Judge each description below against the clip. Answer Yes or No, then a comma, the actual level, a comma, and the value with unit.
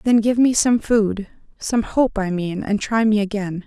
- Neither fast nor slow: Yes, average, 195 wpm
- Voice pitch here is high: Yes, high, 215 Hz